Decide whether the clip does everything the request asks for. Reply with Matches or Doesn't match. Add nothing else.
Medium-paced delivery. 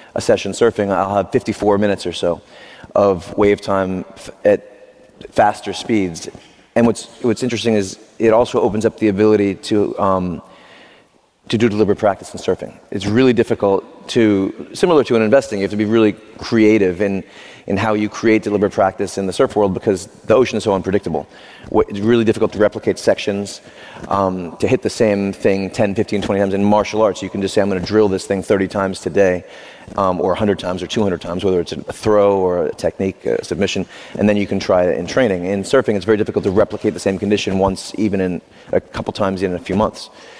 Doesn't match